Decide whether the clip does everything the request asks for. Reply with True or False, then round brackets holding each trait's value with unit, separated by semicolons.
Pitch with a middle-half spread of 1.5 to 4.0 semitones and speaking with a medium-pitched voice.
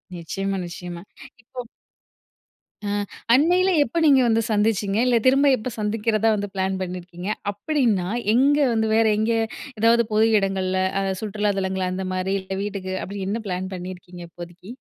False (3.4 semitones; 200 Hz)